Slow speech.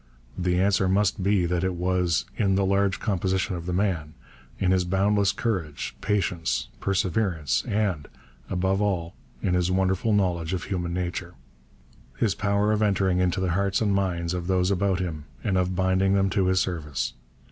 No: average, 170 wpm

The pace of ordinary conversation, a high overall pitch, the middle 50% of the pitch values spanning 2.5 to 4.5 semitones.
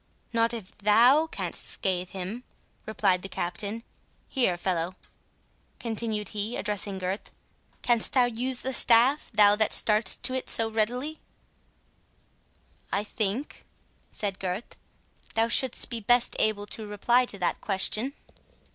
No: slow, 130 wpm; high, 220 Hz; average, 3.2 semitones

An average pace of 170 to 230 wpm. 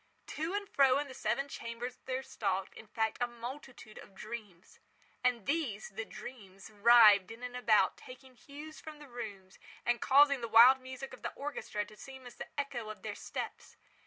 Yes: average, 180 wpm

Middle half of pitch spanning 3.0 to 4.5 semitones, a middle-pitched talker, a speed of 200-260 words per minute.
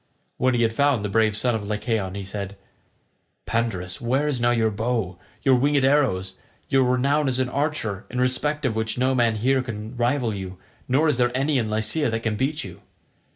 No: average, 3.7 semitones; low, 120 Hz; fast, 205 wpm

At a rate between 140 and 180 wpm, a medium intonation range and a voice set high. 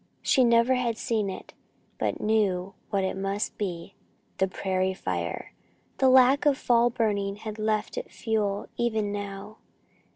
Yes: average, 150 wpm; average, 3.1 semitones; high, 210 Hz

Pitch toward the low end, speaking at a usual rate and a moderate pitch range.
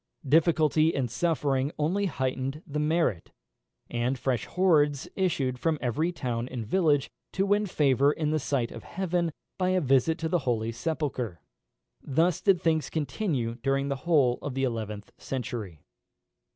No: medium, 145 Hz; average, 150 wpm; average, 4.4 semitones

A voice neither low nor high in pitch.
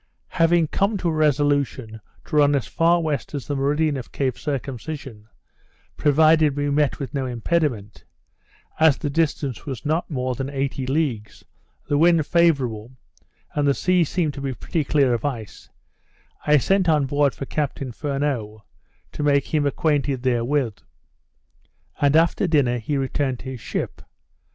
Yes: medium, 145 Hz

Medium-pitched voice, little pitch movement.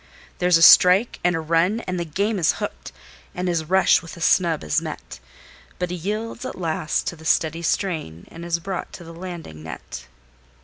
Yes: medium, 170 Hz; narrow, 2.3 semitones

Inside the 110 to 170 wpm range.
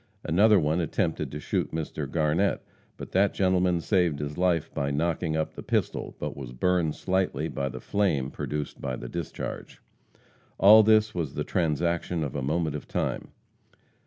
Yes: average, 165 wpm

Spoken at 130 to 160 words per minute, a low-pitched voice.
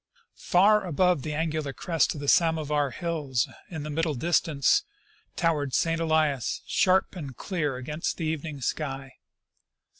No: average, 140 wpm; medium, 155 Hz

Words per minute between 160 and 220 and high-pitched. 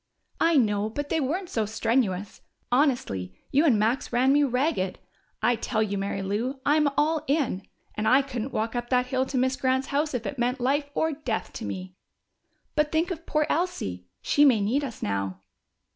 Yes: average, 190 wpm; very high, 255 Hz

